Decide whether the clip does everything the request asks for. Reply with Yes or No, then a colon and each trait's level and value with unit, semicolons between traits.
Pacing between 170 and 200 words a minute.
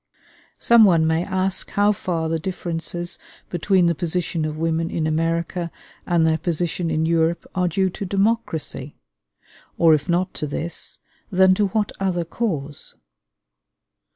No: average, 145 wpm